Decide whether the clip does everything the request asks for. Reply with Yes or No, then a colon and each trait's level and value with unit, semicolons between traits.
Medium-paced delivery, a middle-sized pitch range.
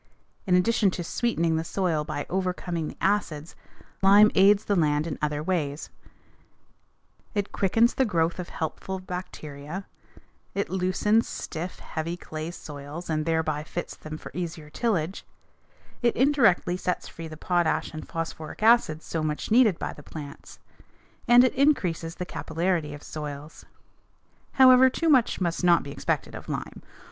Yes: average, 150 wpm; average, 4.1 semitones